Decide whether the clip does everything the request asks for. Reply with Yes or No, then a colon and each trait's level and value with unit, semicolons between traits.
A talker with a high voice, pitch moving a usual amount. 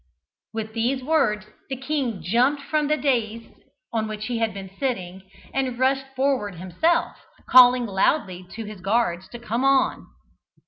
Yes: high, 235 Hz; average, 4.4 semitones